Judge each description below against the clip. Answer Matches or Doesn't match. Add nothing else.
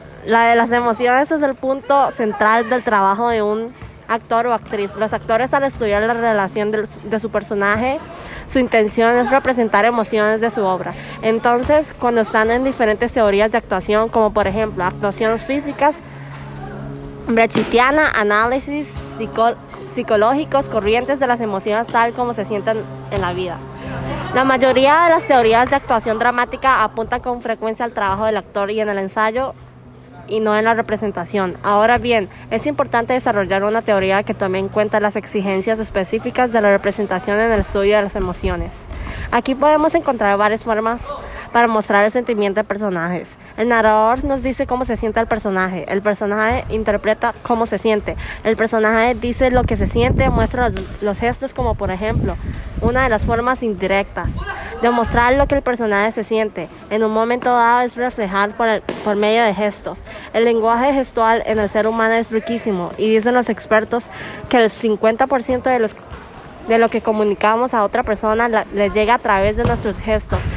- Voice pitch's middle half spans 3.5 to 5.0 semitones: Doesn't match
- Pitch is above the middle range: Matches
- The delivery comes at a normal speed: Matches